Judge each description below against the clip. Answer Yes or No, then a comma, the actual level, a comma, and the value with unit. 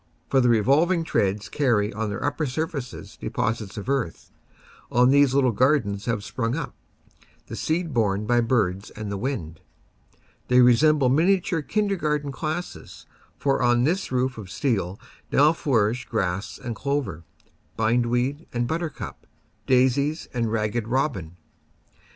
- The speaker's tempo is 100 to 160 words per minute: Yes, average, 140 wpm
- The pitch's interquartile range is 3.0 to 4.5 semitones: No, average, 5.0 semitones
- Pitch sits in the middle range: No, low, 125 Hz